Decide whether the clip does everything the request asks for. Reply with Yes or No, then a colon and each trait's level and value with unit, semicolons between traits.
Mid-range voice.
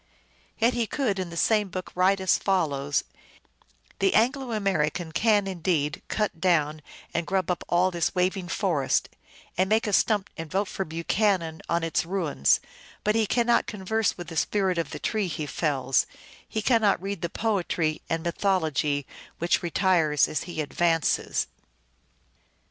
Yes: medium, 180 Hz